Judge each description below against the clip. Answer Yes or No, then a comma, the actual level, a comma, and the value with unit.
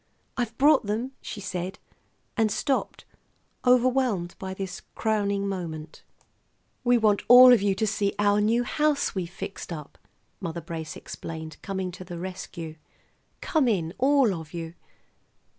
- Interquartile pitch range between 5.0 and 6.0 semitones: Yes, wide, 5.6 semitones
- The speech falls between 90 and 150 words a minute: Yes, slow, 135 wpm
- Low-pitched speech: No, high, 200 Hz